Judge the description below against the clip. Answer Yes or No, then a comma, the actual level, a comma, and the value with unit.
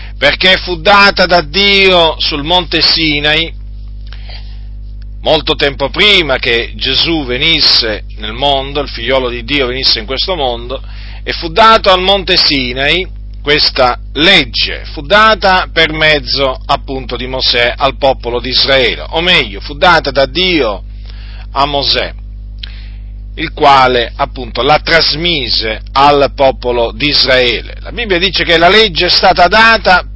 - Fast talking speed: No, average, 135 wpm